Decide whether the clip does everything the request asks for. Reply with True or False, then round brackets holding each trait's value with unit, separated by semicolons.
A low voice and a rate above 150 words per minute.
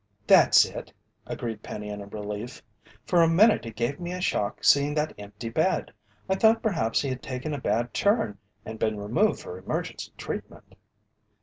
True (125 Hz; 175 wpm)